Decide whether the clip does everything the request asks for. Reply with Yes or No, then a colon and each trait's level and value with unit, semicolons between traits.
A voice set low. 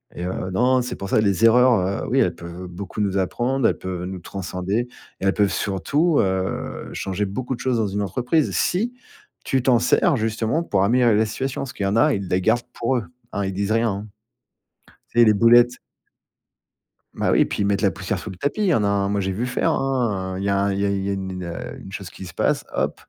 Yes: low, 100 Hz